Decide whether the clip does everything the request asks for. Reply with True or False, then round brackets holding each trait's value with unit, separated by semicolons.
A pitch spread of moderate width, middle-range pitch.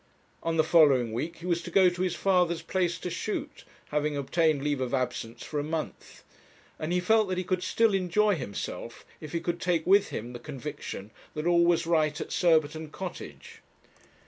True (3.3 semitones; 165 Hz)